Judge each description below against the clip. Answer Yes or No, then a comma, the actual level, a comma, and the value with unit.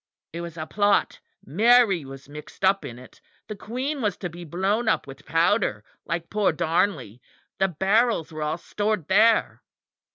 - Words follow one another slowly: No, average, 165 wpm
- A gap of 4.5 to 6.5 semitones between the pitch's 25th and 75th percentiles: Yes, average, 5.3 semitones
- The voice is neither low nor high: Yes, medium, 180 Hz